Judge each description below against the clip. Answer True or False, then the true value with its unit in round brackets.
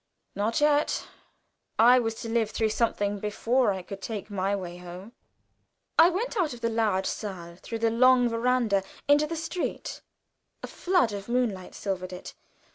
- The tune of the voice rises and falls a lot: False (4.2 semitones)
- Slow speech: False (165 wpm)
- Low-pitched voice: False (225 Hz)